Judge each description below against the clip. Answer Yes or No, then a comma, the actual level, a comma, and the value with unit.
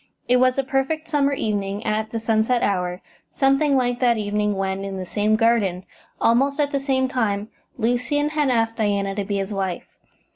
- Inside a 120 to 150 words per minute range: No, average, 185 wpm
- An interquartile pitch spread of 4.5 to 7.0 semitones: Yes, average, 4.8 semitones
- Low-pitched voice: No, high, 225 Hz